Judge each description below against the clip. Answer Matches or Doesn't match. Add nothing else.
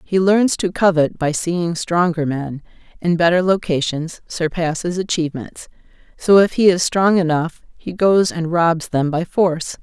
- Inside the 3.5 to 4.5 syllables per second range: Matches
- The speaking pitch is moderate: Matches